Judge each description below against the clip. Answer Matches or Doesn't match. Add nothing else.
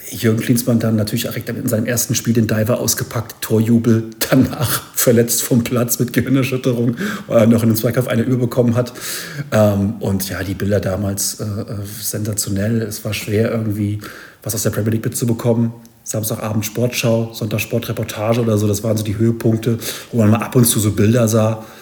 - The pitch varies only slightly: Matches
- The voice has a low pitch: Matches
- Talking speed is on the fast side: Doesn't match